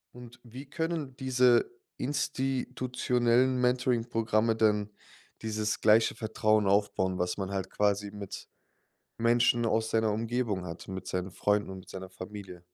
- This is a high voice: No, low, 110 Hz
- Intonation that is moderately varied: Yes, average, 3.4 semitones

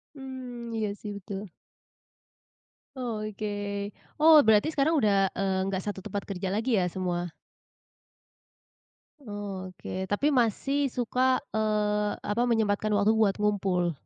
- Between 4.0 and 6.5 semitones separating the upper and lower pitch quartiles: No, average, 3.1 semitones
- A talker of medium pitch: No, high, 210 Hz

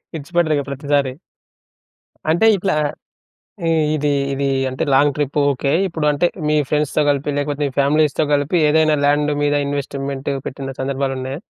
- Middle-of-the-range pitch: Yes, medium, 145 Hz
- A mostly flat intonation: Yes, narrow, 1.6 semitones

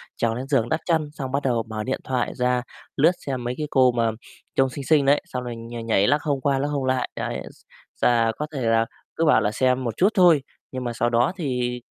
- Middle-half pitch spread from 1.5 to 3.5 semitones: Yes, average, 3.1 semitones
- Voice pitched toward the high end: No, low, 130 Hz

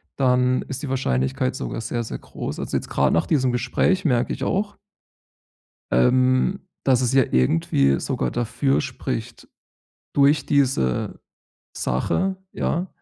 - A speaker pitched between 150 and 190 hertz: No, low, 125 Hz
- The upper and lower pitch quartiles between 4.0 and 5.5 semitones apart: Yes, average, 4.4 semitones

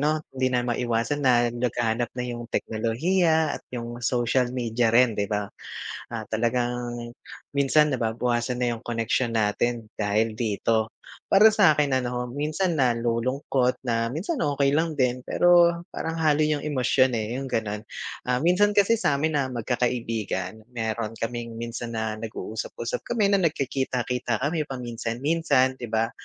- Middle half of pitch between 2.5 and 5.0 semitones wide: Yes, average, 3.9 semitones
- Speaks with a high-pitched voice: No, low, 125 Hz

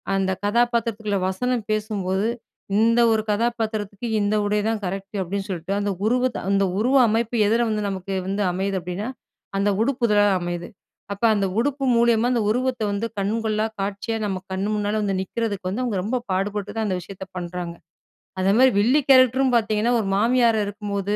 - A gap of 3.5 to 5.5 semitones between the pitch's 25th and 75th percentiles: No, average, 2.9 semitones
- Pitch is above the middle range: Yes, high, 210 Hz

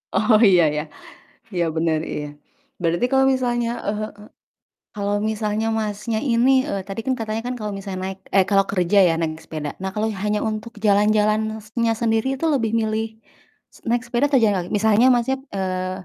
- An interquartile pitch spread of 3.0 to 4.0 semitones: No, narrow, 2.6 semitones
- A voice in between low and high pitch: No, high, 215 Hz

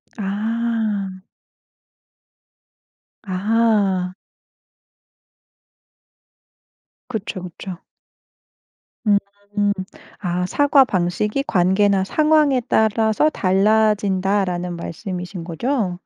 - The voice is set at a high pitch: Yes, high, 205 Hz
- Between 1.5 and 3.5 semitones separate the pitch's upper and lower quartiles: Yes, average, 3.0 semitones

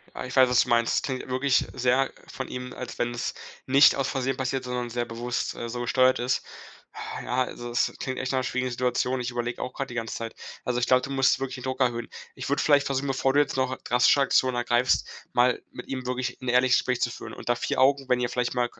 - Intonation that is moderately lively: No, narrow, 1.2 semitones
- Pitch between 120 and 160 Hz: Yes, low, 125 Hz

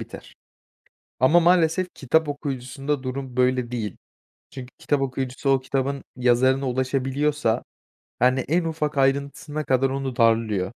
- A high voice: No, low, 135 Hz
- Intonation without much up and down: Yes, narrow, 2.3 semitones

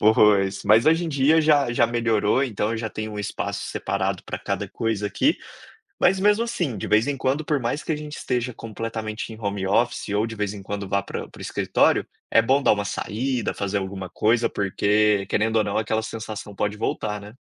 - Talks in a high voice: No, low, 110 Hz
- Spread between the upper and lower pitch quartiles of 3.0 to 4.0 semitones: Yes, average, 3.5 semitones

